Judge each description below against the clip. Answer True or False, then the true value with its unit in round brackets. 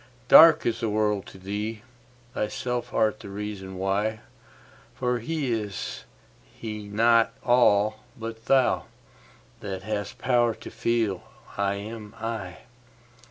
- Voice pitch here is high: False (110 Hz)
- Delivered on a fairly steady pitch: True (2.3 semitones)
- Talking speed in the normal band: False (115 wpm)